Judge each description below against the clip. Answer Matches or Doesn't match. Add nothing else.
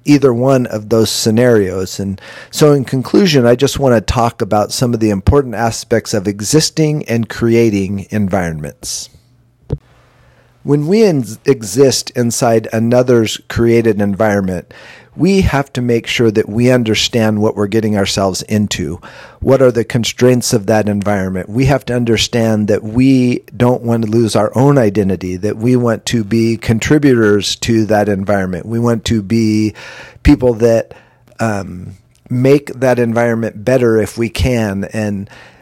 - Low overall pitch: Matches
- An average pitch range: Matches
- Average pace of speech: Matches